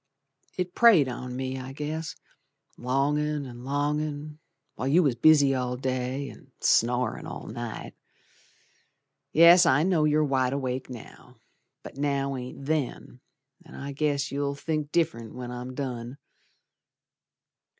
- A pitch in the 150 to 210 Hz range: No, medium, 140 Hz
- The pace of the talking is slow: Yes, slow, 130 wpm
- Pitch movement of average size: Yes, average, 3.0 semitones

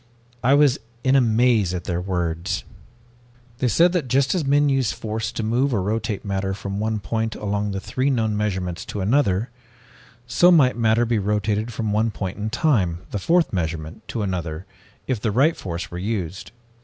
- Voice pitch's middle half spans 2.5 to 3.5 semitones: No, average, 4.4 semitones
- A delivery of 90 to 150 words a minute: No, average, 185 wpm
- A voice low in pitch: Yes, low, 110 Hz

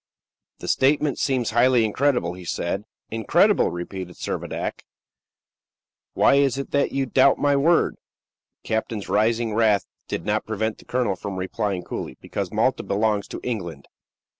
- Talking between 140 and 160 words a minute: Yes, average, 145 wpm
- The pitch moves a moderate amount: Yes, average, 4.8 semitones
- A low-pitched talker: Yes, low, 110 Hz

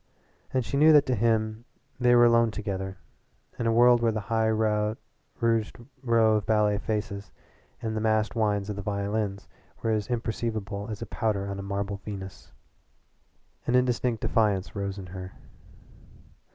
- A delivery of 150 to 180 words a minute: Yes, average, 155 wpm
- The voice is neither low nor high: No, low, 110 Hz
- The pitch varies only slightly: Yes, narrow, 2.3 semitones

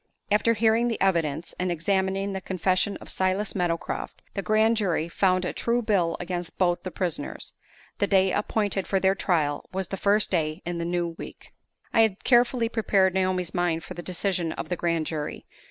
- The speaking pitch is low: No, medium, 185 Hz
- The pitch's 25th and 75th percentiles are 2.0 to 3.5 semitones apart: Yes, average, 2.7 semitones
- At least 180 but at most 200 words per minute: Yes, average, 185 wpm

